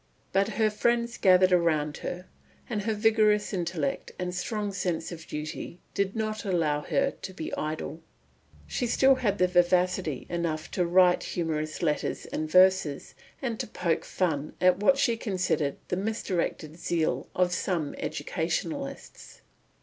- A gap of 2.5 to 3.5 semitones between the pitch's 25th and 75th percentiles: No, average, 4.4 semitones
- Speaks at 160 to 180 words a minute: No, average, 140 wpm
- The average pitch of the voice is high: No, medium, 180 Hz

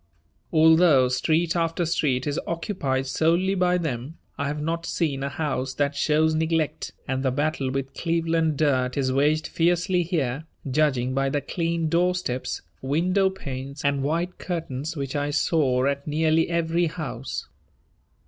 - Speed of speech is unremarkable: Yes, average, 150 wpm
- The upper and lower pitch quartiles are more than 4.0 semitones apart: No, average, 3.5 semitones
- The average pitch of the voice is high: No, medium, 155 Hz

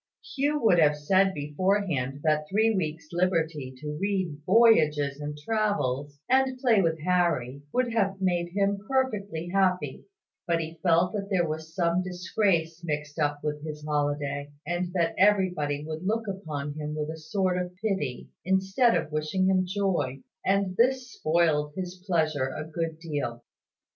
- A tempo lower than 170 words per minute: Yes, average, 155 wpm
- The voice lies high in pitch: No, medium, 170 Hz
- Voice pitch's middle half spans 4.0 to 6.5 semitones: Yes, average, 4.5 semitones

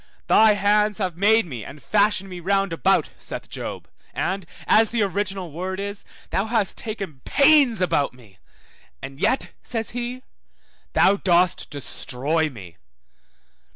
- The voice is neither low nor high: No, high, 195 Hz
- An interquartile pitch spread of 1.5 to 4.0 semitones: No, average, 4.6 semitones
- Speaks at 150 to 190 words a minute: No, slow, 135 wpm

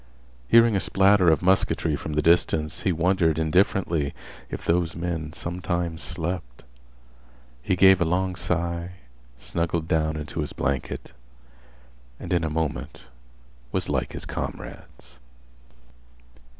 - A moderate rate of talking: No, slow, 125 wpm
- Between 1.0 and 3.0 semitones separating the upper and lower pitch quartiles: Yes, narrow, 2.4 semitones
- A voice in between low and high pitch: No, very low, 85 Hz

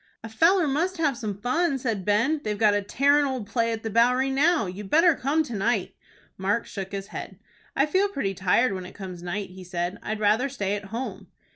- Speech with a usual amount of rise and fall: No, wide, 5.8 semitones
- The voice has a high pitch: Yes, high, 225 Hz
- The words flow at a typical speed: No, fast, 220 wpm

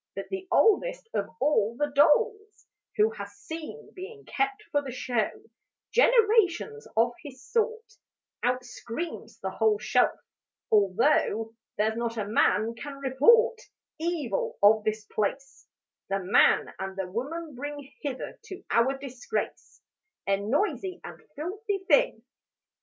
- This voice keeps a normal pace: No, slow, 130 wpm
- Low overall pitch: No, very high, 290 Hz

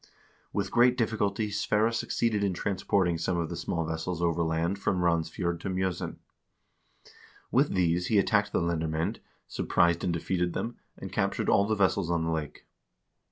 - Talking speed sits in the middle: Yes, average, 160 wpm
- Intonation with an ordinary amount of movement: Yes, average, 3.1 semitones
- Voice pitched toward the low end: Yes, very low, 90 Hz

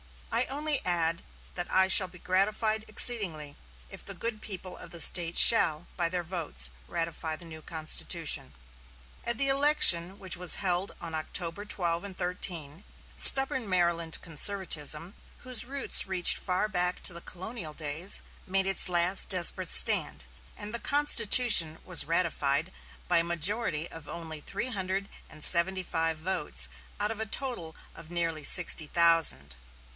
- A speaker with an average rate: Yes, average, 150 wpm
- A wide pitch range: No, average, 3.7 semitones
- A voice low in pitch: No, medium, 180 Hz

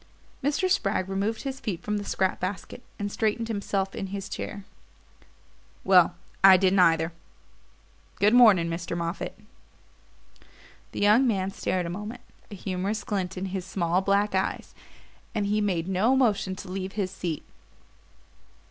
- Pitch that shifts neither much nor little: No, narrow, 2.3 semitones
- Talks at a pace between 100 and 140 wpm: No, average, 150 wpm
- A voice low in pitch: No, high, 195 Hz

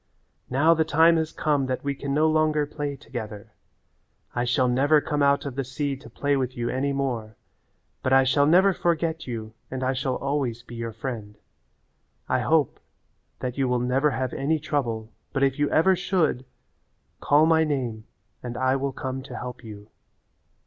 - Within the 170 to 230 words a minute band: Yes, average, 185 wpm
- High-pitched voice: No, low, 135 Hz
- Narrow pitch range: No, average, 3.1 semitones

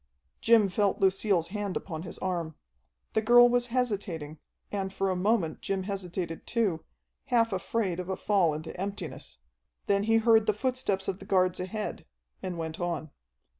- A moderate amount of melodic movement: Yes, average, 3.6 semitones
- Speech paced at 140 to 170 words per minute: Yes, average, 165 wpm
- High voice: Yes, high, 195 Hz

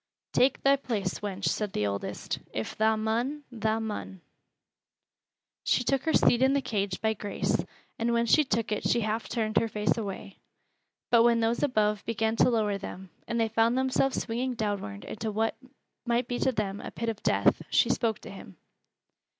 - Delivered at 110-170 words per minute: No, average, 185 wpm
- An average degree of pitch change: No, narrow, 2.3 semitones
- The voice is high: Yes, high, 225 Hz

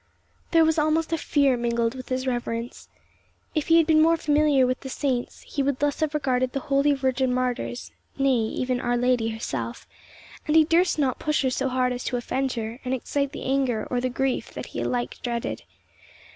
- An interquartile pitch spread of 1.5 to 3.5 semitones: Yes, average, 2.9 semitones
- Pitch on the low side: No, very high, 260 Hz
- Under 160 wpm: No, average, 200 wpm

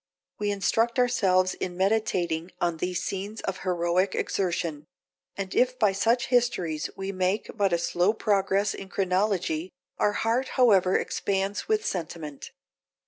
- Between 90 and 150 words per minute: Yes, average, 140 wpm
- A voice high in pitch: Yes, high, 195 Hz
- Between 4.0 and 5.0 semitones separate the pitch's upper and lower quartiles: No, average, 2.9 semitones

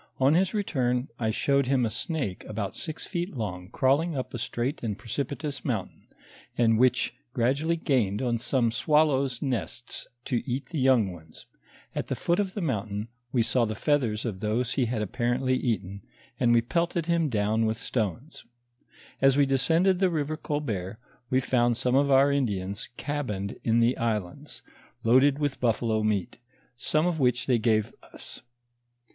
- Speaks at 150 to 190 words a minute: Yes, average, 165 wpm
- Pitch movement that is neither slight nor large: Yes, average, 4.4 semitones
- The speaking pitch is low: Yes, low, 125 Hz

